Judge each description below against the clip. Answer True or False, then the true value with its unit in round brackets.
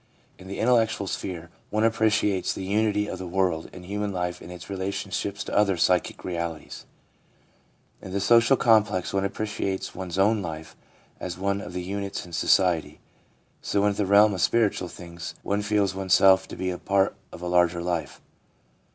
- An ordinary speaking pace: True (175 wpm)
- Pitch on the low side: True (95 Hz)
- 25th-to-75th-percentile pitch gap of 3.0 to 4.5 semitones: False (2.6 semitones)